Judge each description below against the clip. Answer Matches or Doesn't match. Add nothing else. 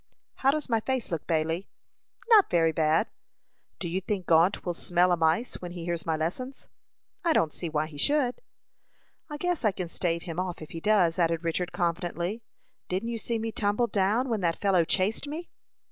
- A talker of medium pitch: Matches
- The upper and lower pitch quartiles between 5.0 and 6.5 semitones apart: Matches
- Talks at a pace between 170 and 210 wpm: Matches